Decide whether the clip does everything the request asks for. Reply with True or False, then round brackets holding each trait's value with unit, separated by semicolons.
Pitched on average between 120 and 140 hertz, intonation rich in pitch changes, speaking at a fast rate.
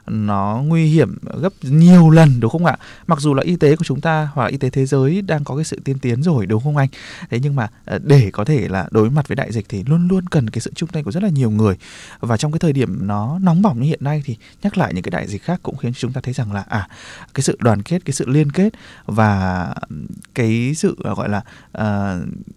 True (135 Hz; 6.2 semitones; 260 wpm)